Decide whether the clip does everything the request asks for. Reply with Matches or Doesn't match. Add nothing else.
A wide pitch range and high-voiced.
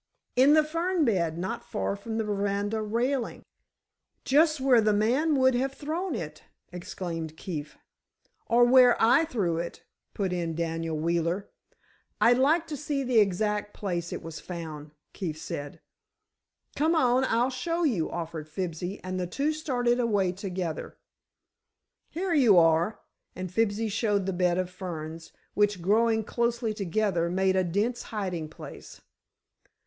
Matches